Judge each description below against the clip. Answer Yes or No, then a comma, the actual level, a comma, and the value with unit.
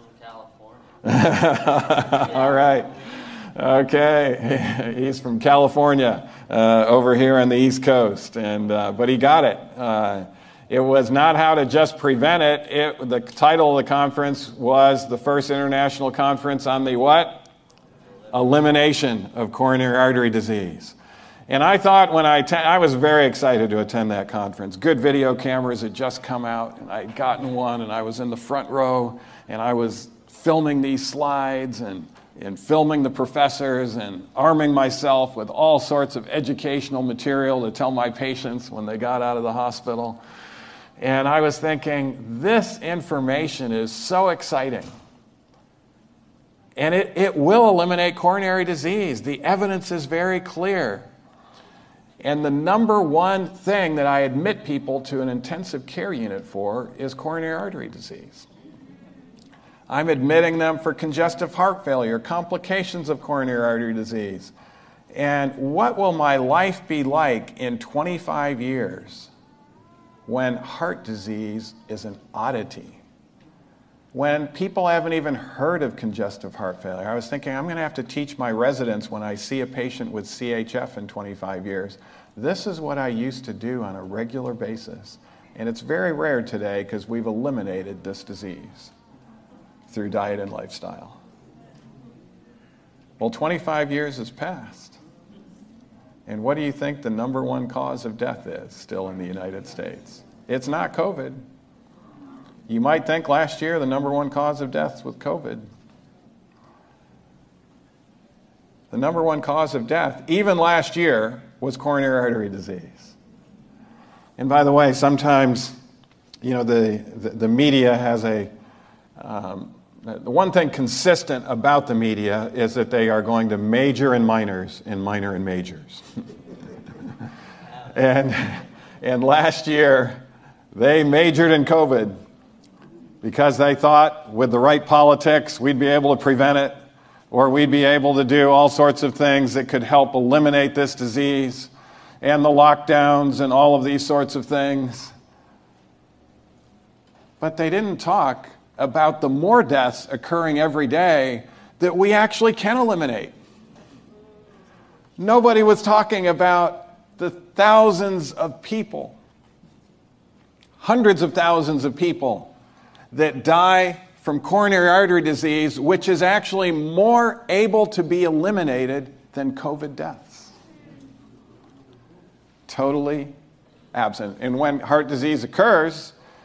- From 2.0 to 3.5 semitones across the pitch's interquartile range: No, average, 4.3 semitones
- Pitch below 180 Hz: Yes, medium, 140 Hz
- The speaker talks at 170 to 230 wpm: No, average, 145 wpm